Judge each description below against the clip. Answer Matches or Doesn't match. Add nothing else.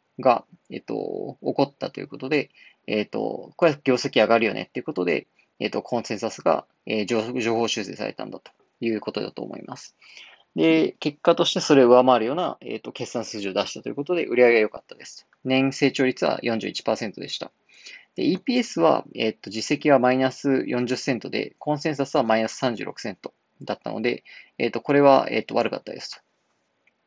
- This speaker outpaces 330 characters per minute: Matches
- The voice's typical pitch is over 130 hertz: Doesn't match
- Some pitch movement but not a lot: Matches